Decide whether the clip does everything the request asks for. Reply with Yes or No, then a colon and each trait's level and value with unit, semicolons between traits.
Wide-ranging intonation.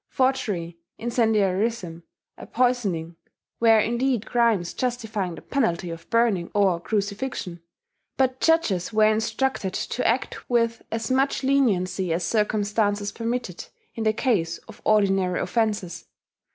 No: average, 4.5 semitones